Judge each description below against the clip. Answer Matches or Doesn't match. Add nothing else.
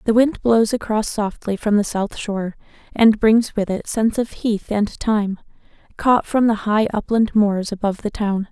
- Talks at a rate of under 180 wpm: Doesn't match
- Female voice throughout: Matches